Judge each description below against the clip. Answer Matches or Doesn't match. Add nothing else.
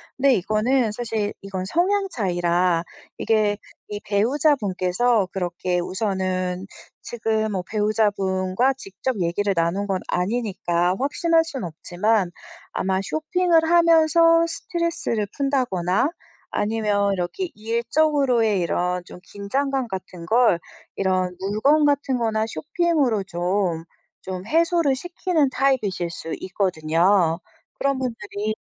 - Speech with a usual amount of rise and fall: Doesn't match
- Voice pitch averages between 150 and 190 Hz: Doesn't match